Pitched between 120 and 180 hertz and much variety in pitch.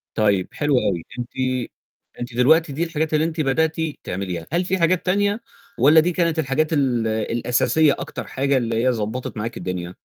Yes: low, 135 Hz; wide, 5.9 semitones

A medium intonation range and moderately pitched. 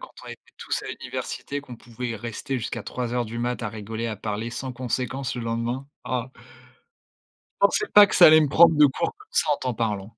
No: average, 3.1 semitones; low, 125 Hz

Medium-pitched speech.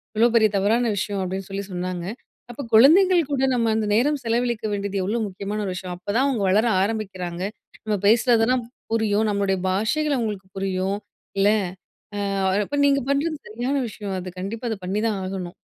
No: high, 210 Hz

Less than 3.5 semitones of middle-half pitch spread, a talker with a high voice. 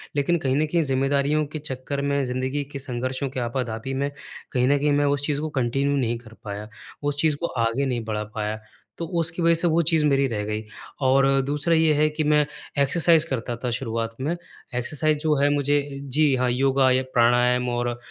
No: average, 3.1 semitones; low, 135 Hz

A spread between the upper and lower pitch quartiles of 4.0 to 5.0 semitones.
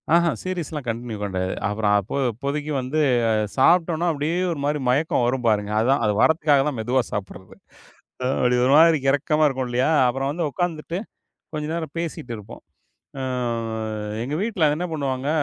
Yes: average, 4.5 semitones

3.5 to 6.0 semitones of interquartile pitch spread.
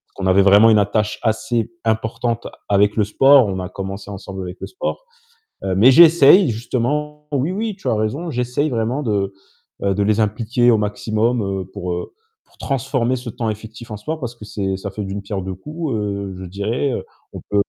Yes: average, 3.9 semitones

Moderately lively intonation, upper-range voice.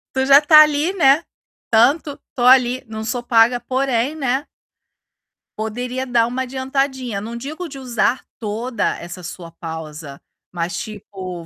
Yes: average, 4.0 semitones; high, 245 Hz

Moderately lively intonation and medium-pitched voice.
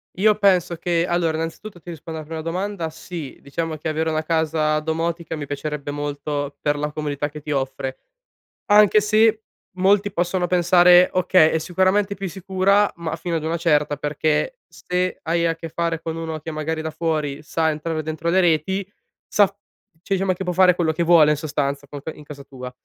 Yes: average, 3.0 semitones; medium, 165 Hz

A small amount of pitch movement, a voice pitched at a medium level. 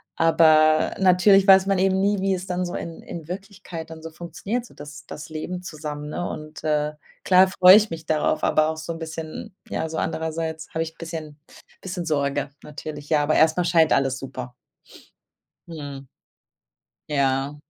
No: average, 3.2 semitones; medium, 160 Hz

